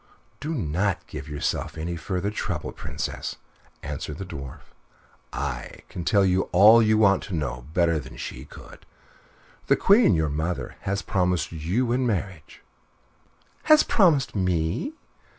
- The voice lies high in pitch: No, very low, 90 Hz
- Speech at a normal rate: Yes, average, 145 wpm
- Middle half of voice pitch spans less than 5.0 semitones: No, average, 5.3 semitones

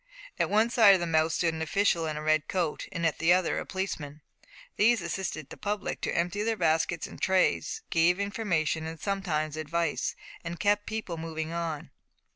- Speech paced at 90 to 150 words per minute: No, average, 180 wpm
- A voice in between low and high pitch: Yes, medium, 170 Hz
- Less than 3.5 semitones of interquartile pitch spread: No, average, 3.8 semitones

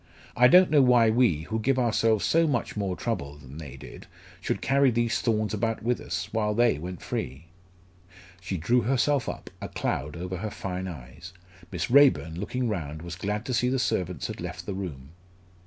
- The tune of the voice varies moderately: No, wide, 6.1 semitones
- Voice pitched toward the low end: Yes, low, 105 Hz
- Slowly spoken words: No, average, 190 wpm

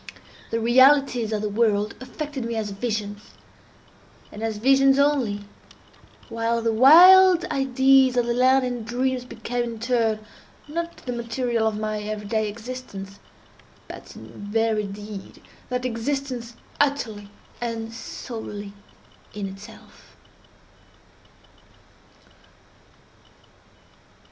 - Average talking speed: No, slow, 110 wpm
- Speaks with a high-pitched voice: Yes, high, 230 Hz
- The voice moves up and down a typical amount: Yes, average, 3.3 semitones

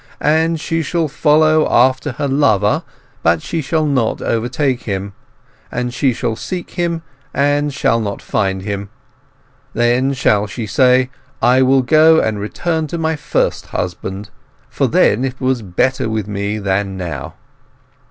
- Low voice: Yes, low, 125 Hz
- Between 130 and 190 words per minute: Yes, average, 150 wpm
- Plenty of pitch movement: Yes, wide, 6.3 semitones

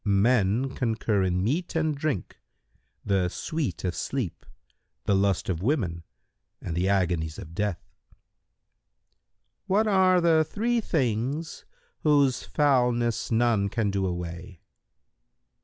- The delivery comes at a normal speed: No, slow, 120 wpm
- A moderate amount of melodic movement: No, wide, 7.6 semitones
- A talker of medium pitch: No, low, 115 Hz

